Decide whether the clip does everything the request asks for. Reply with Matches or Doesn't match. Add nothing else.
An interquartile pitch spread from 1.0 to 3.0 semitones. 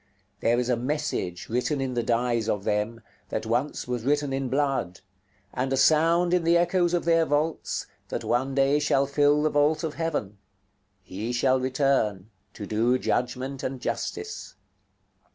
Doesn't match